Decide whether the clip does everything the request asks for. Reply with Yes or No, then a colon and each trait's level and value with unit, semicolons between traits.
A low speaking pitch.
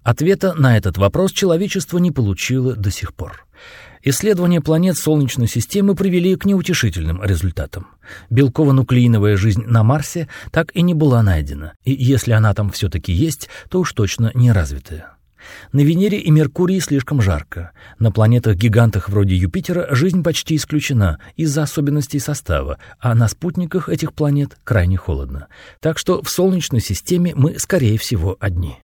Yes: low, 125 Hz